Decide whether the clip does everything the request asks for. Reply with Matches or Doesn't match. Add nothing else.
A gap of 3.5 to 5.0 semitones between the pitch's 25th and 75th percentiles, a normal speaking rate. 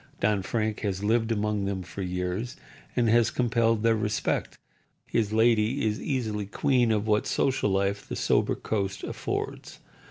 Doesn't match